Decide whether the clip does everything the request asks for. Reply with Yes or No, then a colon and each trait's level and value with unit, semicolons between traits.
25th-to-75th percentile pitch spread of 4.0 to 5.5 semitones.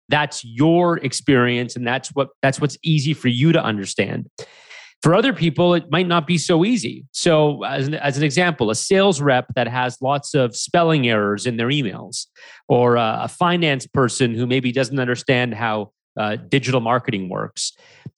Yes: average, 4.8 semitones